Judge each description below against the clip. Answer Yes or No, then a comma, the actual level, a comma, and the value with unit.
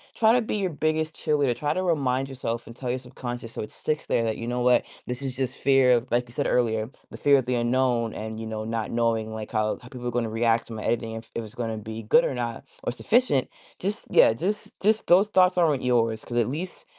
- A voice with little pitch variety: No, average, 4.0 semitones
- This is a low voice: Yes, low, 125 Hz